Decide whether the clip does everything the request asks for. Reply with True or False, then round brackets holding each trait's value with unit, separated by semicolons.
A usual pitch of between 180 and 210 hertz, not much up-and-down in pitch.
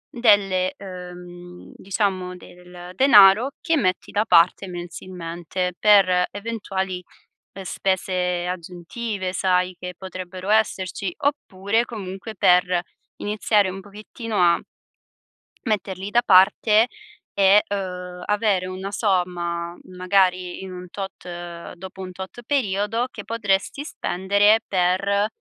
True (190 Hz; 2.3 semitones)